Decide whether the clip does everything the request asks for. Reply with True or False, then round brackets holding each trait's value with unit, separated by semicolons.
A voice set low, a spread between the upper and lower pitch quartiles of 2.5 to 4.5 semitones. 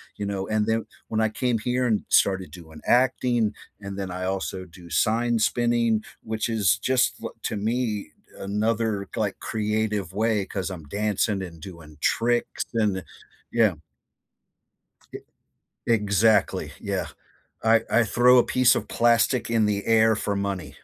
True (110 Hz; 2.8 semitones)